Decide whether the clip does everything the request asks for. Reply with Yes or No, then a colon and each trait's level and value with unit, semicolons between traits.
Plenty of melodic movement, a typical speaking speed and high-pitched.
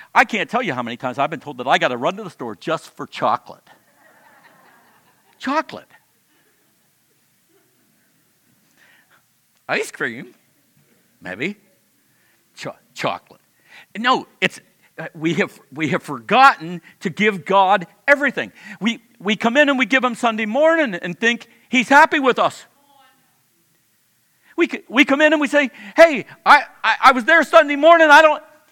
Yes: wide, 7.2 semitones; average, 150 wpm; high, 245 Hz